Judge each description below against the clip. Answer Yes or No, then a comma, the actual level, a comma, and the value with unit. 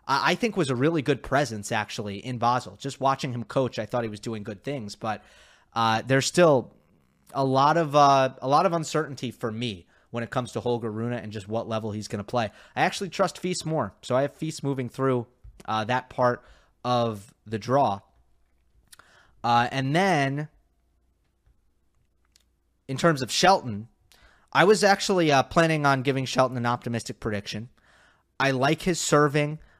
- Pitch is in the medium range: No, low, 125 Hz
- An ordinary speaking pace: Yes, average, 175 wpm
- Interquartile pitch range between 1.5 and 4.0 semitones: No, average, 4.6 semitones